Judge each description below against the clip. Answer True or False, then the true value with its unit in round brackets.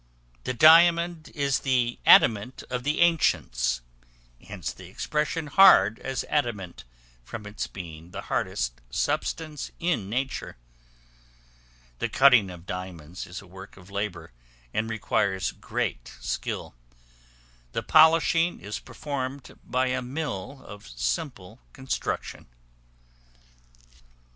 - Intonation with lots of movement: True (7.7 semitones)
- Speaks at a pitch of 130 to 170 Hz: False (120 Hz)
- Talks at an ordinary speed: False (110 wpm)